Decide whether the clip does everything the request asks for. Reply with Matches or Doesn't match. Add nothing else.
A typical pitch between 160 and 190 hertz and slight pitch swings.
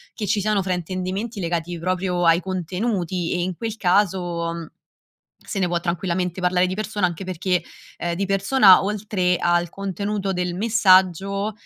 Matches